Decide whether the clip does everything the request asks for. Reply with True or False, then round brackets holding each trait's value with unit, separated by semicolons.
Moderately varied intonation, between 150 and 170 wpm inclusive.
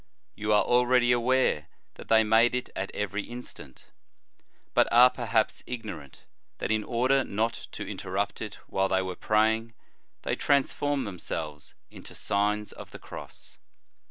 True (3.5 semitones; 155 wpm)